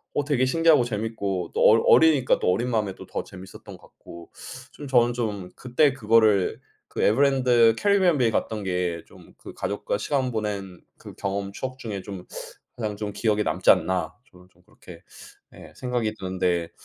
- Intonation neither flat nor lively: Yes, average, 4.7 semitones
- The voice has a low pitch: Yes, low, 110 Hz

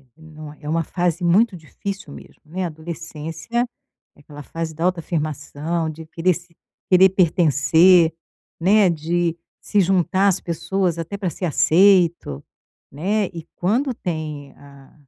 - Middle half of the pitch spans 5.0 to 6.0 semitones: No, average, 2.9 semitones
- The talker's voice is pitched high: No, medium, 170 Hz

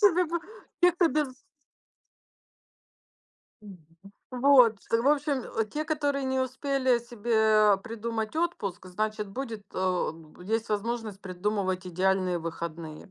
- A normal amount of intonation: No, wide, 6.0 semitones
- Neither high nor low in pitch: No, high, 225 Hz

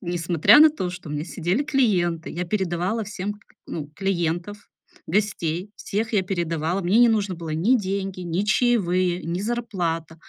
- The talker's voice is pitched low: No, medium, 185 Hz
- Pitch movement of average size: Yes, average, 3.5 semitones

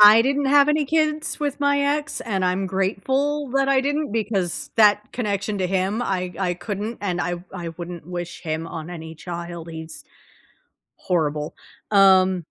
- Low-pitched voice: No, high, 195 Hz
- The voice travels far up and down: Yes, wide, 7.3 semitones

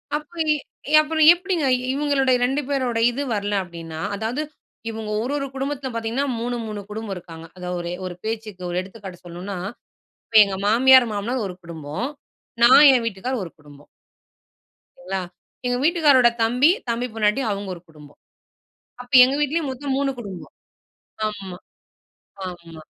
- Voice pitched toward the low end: No, high, 225 Hz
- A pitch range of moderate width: No, wide, 6.3 semitones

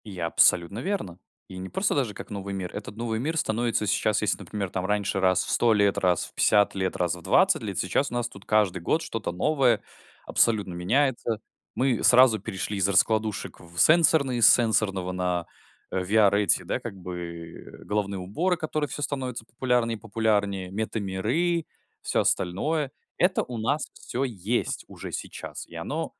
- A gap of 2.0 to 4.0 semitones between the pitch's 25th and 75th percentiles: No, average, 4.7 semitones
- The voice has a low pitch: Yes, low, 105 Hz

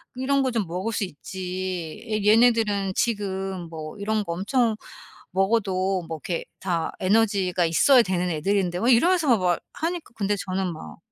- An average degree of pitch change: Yes, average, 3.8 semitones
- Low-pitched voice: No, high, 195 Hz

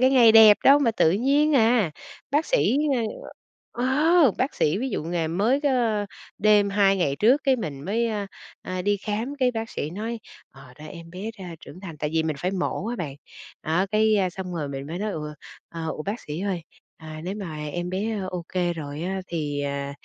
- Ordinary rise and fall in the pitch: No, wide, 5.7 semitones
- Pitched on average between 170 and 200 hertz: Yes, high, 195 Hz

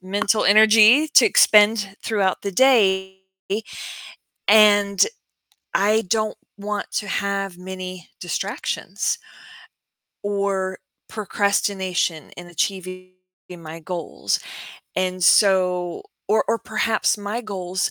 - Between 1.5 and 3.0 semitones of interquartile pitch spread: Yes, narrow, 2.4 semitones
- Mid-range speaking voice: No, high, 200 Hz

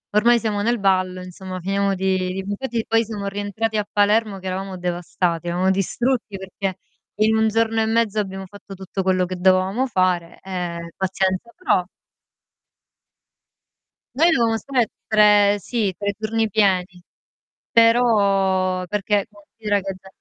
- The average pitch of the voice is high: Yes, high, 200 Hz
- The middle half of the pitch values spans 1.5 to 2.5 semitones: No, average, 2.9 semitones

